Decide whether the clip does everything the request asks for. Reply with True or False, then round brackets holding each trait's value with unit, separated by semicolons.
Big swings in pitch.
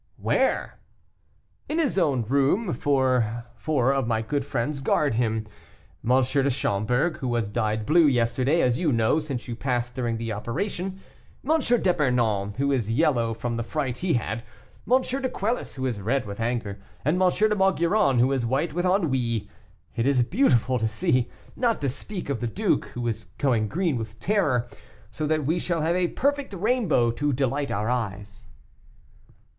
True (6.1 semitones)